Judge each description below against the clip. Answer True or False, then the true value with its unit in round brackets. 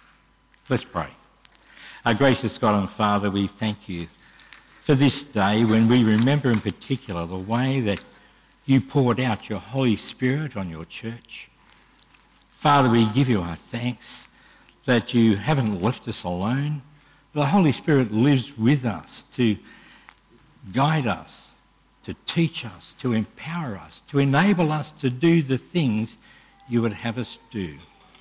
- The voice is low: True (120 Hz)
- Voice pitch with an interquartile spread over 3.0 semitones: True (4.4 semitones)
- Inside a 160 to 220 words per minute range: False (145 wpm)